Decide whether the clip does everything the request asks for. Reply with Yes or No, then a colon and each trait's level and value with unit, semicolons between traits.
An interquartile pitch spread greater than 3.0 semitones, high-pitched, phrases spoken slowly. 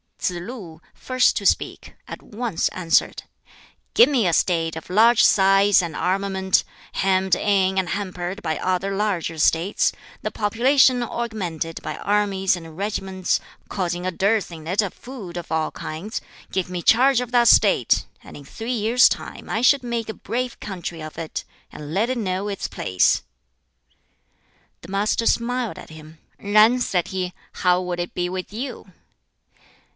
No: average, 4.1 semitones; high, 195 Hz; average, 160 wpm